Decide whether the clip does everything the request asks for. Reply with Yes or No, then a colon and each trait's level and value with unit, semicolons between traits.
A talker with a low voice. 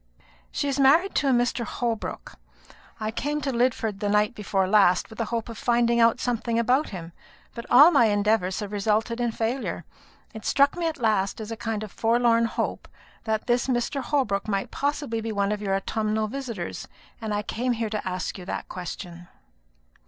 No: high, 225 Hz